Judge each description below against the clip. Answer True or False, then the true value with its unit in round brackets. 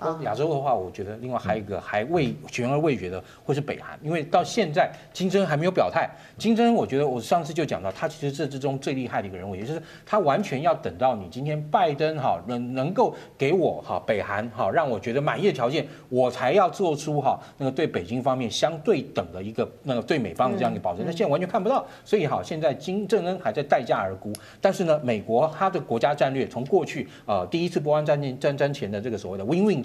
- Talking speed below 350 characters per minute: False (375 characters per minute)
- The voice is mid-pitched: True (150 Hz)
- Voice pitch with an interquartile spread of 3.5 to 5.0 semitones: False (5.5 semitones)